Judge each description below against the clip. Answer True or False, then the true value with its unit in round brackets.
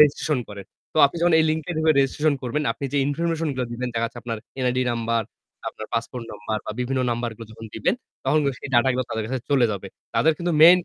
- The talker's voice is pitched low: True (125 Hz)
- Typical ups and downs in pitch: True (4.8 semitones)